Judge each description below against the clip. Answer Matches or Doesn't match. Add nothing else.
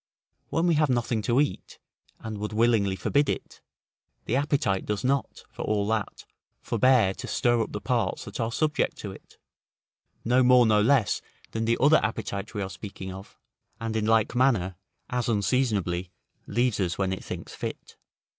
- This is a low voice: Matches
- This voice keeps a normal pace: Matches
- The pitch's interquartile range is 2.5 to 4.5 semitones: Matches